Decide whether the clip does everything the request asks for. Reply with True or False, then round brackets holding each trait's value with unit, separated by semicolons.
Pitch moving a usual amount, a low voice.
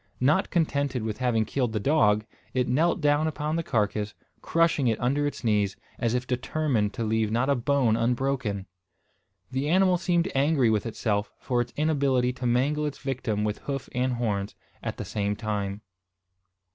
True (4.8 semitones; 125 Hz)